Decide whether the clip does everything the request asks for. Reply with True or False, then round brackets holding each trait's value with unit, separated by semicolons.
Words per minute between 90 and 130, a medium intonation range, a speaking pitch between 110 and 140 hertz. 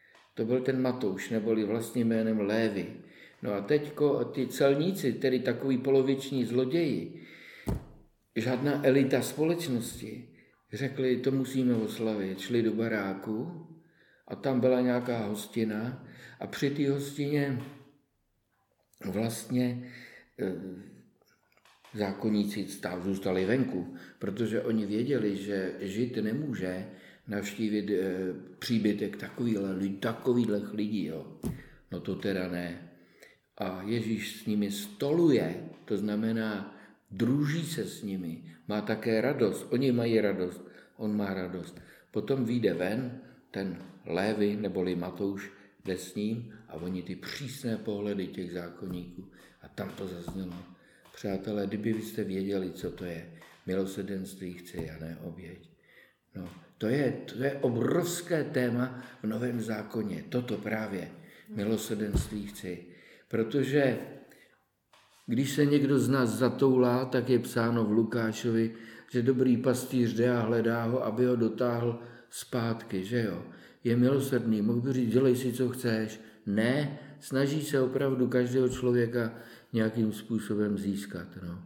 True (120 wpm; 4.1 semitones; 115 Hz)